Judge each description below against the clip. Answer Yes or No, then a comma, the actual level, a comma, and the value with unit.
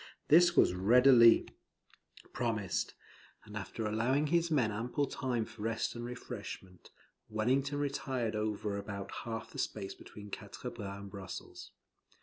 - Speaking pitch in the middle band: No, low, 115 Hz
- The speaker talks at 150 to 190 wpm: No, slow, 135 wpm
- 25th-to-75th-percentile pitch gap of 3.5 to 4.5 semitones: Yes, average, 4.0 semitones